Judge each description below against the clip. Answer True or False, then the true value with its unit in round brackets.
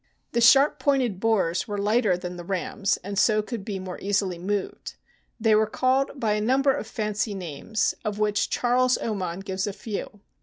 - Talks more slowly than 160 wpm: False (185 wpm)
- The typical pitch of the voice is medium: False (210 Hz)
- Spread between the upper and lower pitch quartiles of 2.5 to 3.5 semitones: True (3.2 semitones)